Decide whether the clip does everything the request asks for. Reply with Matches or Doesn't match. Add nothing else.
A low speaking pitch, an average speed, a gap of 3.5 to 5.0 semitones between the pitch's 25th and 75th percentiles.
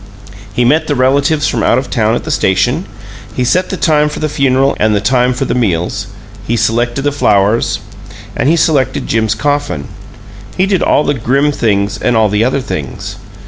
Matches